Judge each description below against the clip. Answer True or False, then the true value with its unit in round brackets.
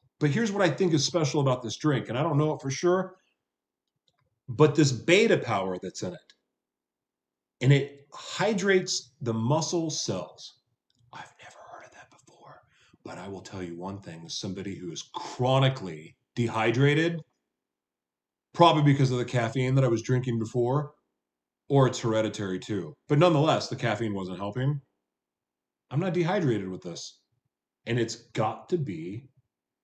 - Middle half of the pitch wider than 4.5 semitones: True (5.6 semitones)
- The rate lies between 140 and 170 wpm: True (155 wpm)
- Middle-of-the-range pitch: False (130 Hz)